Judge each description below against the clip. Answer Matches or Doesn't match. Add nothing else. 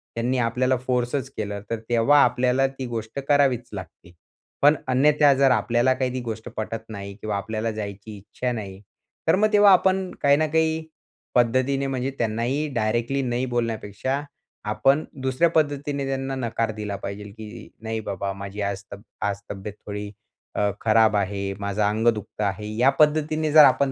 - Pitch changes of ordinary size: Matches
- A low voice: Matches